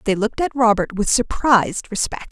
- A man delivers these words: No, female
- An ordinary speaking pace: Yes, average, 180 wpm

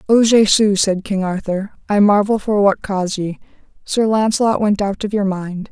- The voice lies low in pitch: No, high, 200 Hz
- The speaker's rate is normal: Yes, average, 190 wpm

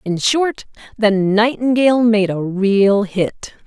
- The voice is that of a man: No, female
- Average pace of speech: No, slow, 130 wpm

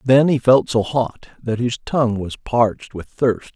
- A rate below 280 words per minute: Yes, average, 200 wpm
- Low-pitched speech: Yes, low, 120 Hz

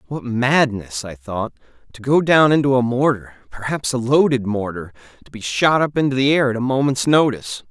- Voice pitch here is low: Yes, low, 125 Hz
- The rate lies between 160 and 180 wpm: No, average, 195 wpm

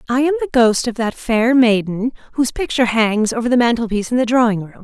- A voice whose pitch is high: Yes, high, 235 Hz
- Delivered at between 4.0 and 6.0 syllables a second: No, 6.3 syllables/s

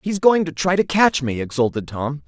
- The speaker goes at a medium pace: No, fast, 240 wpm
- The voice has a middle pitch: Yes, medium, 155 Hz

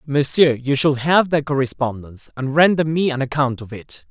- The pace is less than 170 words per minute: No, average, 190 wpm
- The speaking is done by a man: Yes, male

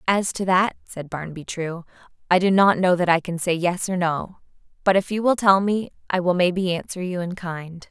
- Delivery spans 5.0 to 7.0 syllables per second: Yes, 5.1 syllables/s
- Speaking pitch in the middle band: Yes, medium, 180 Hz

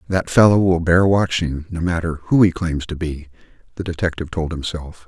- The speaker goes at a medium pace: Yes, average, 190 wpm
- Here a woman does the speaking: No, male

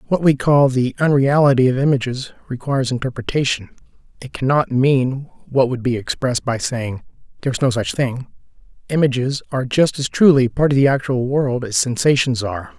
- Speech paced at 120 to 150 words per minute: No, average, 165 wpm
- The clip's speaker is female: No, male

